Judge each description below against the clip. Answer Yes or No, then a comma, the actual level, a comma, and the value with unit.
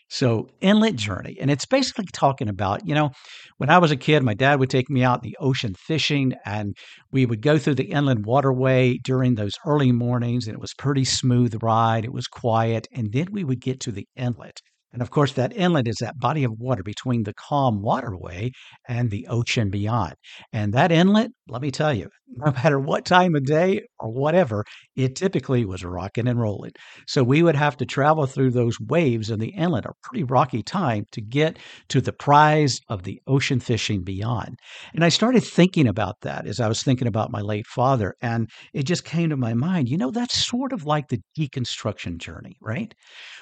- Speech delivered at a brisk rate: Yes, fast, 210 wpm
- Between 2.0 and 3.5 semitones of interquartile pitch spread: No, average, 4.6 semitones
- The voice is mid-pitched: No, low, 130 Hz